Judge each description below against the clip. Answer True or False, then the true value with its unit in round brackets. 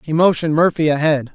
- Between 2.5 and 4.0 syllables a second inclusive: False (6.4 syllables/s)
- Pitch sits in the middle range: True (155 Hz)